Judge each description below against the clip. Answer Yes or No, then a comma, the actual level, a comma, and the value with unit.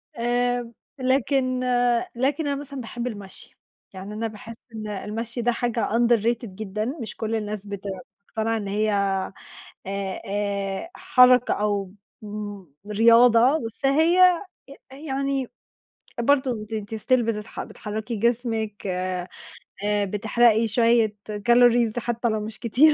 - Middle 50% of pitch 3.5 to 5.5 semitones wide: No, average, 3.0 semitones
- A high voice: Yes, high, 225 Hz